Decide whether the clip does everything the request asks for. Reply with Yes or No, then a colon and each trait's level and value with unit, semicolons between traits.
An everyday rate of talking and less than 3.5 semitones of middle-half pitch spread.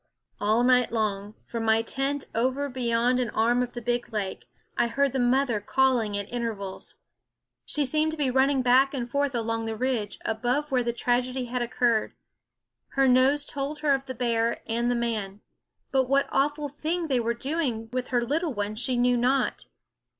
Yes: average, 185 wpm; average, 2.8 semitones